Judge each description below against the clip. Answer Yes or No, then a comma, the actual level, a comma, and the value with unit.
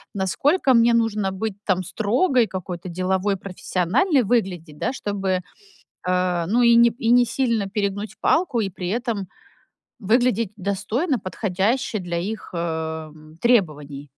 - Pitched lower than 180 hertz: No, high, 200 Hz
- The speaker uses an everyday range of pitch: Yes, average, 4.4 semitones